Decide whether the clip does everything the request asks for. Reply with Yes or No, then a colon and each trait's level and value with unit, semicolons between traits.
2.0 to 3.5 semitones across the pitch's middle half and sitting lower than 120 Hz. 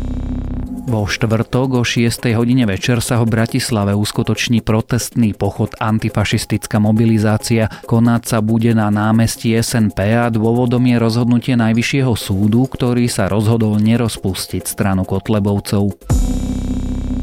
Yes: narrow, 2.4 semitones; low, 110 Hz